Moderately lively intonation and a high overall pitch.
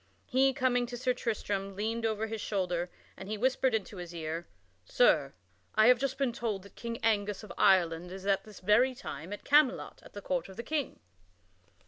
Yes: average, 4.5 semitones; high, 215 Hz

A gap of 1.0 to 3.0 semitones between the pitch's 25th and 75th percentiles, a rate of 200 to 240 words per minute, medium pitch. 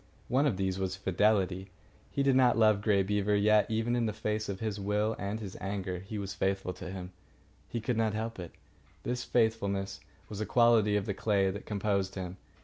No: narrow, 2.4 semitones; fast, 205 wpm; low, 105 Hz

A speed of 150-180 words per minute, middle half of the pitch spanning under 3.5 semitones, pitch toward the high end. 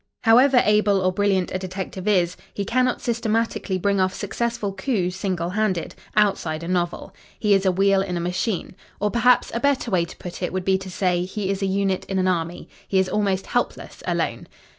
No: fast, 205 wpm; narrow, 2.4 semitones; high, 195 Hz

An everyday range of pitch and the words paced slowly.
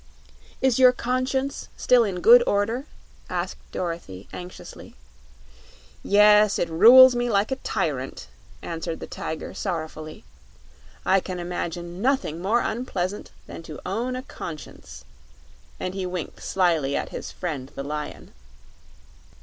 No: wide, 6.4 semitones; slow, 125 wpm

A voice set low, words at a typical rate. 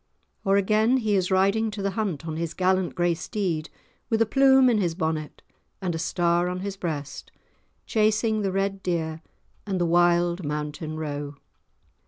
No: medium, 185 Hz; average, 170 wpm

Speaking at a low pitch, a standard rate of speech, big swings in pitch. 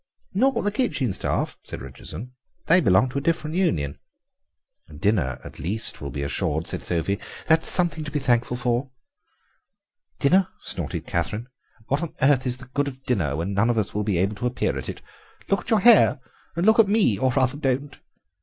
Yes: low, 130 Hz; average, 190 wpm; wide, 7.8 semitones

